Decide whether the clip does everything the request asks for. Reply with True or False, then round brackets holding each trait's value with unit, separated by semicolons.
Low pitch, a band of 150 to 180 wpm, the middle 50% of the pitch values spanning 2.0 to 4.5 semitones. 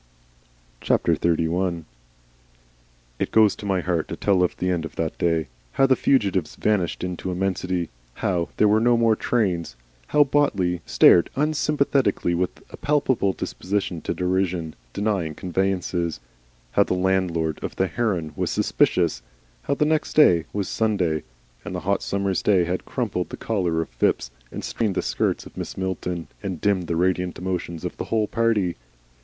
True (95 Hz; 160 wpm; 3.5 semitones)